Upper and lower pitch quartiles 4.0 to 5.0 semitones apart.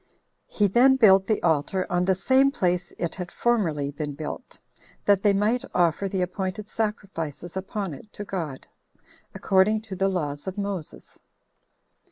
No: average, 3.2 semitones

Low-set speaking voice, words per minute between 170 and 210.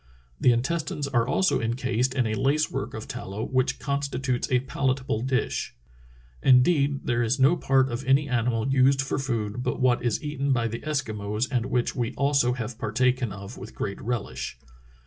Yes: low, 130 Hz; average, 175 wpm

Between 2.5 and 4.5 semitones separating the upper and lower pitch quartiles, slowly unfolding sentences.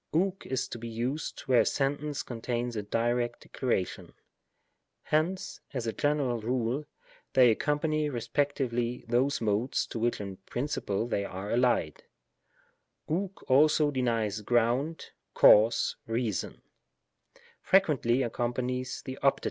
Yes: average, 3.6 semitones; slow, 125 wpm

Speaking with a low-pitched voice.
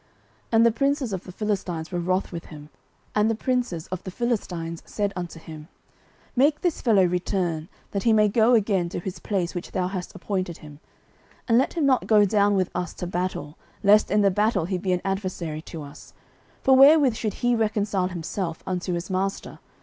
No: high, 190 Hz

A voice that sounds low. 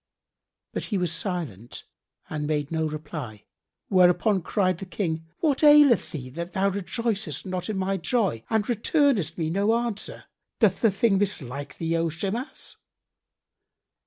No: medium, 185 Hz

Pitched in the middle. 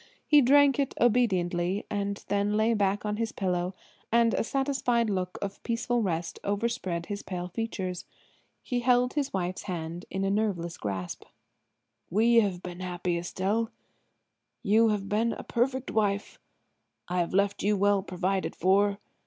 No: high, 200 Hz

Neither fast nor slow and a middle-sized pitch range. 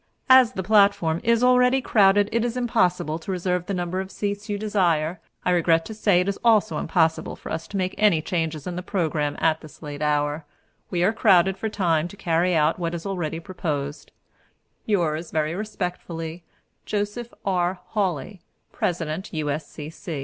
Yes: average, 170 wpm; average, 4.0 semitones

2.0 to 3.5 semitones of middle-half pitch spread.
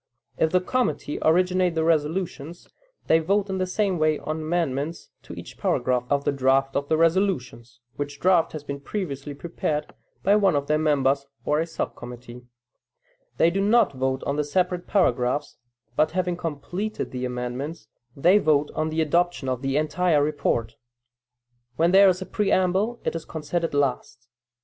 No: average, 4.4 semitones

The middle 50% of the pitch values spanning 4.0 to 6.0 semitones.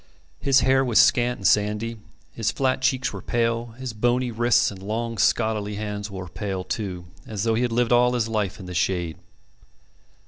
No: average, 3.0 semitones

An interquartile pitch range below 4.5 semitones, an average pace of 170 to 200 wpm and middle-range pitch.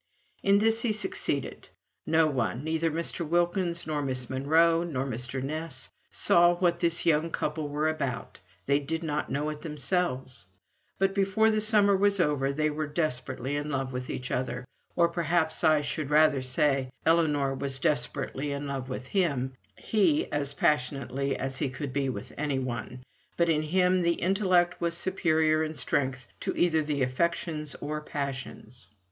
No: average, 4.0 semitones; average, 160 wpm; medium, 150 Hz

